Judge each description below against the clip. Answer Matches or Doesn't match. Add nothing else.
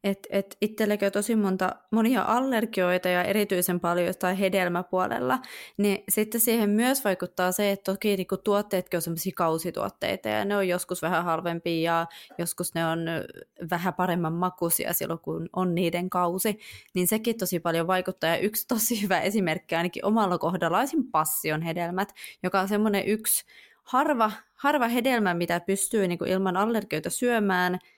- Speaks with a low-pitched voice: Doesn't match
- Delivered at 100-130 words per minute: Doesn't match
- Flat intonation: Doesn't match